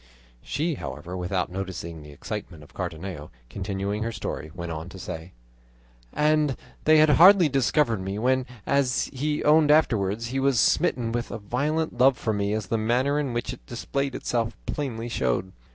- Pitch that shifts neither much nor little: No, wide, 6.8 semitones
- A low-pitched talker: Yes, low, 115 Hz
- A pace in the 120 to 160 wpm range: No, average, 170 wpm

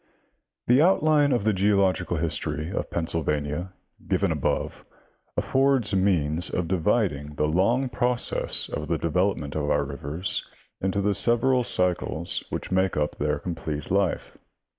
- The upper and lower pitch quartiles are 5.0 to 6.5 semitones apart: Yes, average, 5.3 semitones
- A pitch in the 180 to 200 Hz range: No, very low, 90 Hz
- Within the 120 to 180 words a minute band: Yes, average, 140 wpm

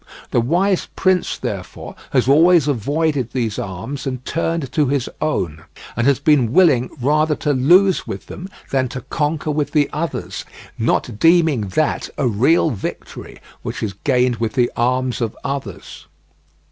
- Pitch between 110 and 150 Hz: Yes, medium, 140 Hz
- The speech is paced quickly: No, average, 155 wpm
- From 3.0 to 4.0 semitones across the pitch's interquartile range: No, average, 4.4 semitones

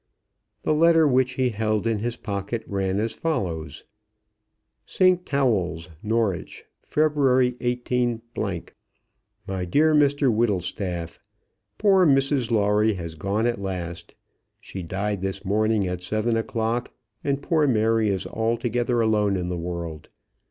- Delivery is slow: Yes, slow, 125 wpm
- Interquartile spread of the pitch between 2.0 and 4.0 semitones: No, average, 4.5 semitones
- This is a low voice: Yes, low, 110 Hz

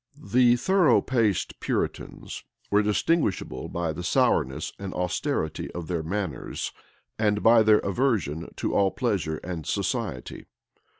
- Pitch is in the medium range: No, low, 100 Hz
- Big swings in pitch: Yes, wide, 5.7 semitones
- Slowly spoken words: Yes, slow, 125 wpm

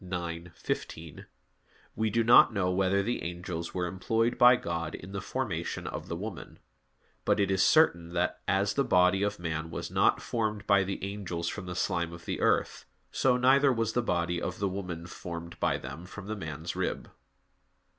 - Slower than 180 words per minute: No, average, 185 wpm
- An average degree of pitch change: Yes, average, 3.7 semitones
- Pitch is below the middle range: Yes, very low, 95 Hz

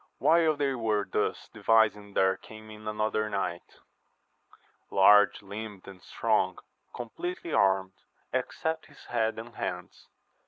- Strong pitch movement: No, average, 2.7 semitones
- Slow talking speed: Yes, slow, 120 wpm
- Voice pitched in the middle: No, low, 110 Hz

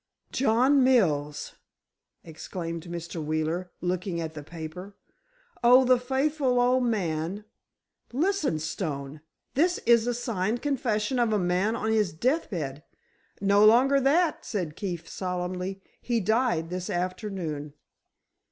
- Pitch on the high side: Yes, high, 195 Hz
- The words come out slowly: Yes, slow, 125 wpm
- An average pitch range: No, wide, 6.5 semitones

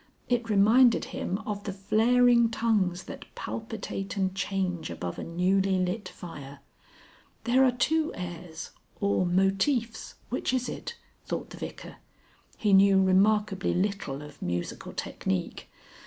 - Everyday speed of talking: No, slow, 130 wpm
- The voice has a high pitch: Yes, high, 195 Hz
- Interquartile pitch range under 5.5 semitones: Yes, average, 4.1 semitones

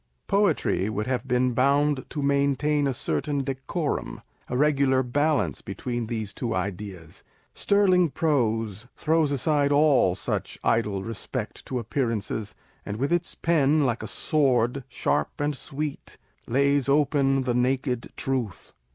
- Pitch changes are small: No, average, 4.1 semitones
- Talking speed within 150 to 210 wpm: No, slow, 135 wpm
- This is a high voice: No, low, 135 Hz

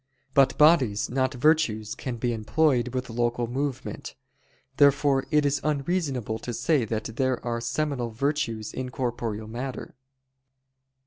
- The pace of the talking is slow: Yes, slow, 130 wpm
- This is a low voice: Yes, low, 130 Hz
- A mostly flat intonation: No, average, 3.3 semitones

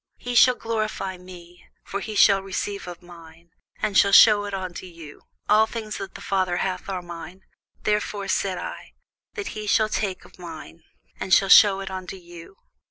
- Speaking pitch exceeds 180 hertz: Yes, high, 190 Hz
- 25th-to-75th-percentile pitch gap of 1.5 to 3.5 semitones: Yes, average, 2.8 semitones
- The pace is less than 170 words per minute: No, average, 180 wpm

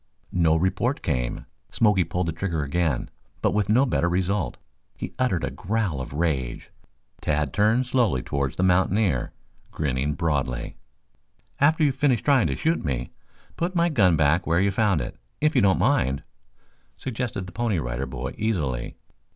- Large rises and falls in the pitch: Yes, wide, 7.7 semitones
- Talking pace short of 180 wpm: Yes, average, 165 wpm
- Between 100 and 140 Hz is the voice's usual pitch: No, very low, 90 Hz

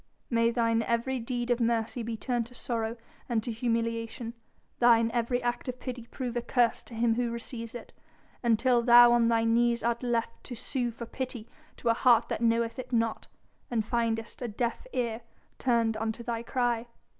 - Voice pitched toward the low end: No, high, 235 Hz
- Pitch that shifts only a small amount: Yes, narrow, 1.1 semitones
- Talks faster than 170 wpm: Yes, average, 185 wpm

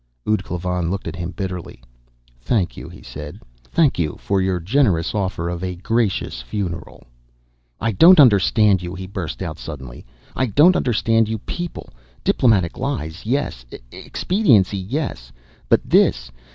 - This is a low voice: Yes, very low, 95 Hz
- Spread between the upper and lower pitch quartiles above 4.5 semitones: Yes, average, 4.9 semitones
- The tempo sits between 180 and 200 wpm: No, average, 145 wpm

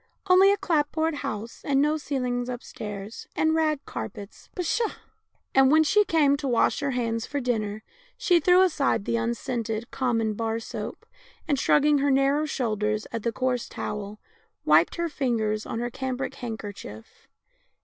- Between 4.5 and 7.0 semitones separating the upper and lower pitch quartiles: Yes, average, 5.0 semitones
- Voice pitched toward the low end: No, very high, 250 Hz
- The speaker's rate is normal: Yes, average, 165 wpm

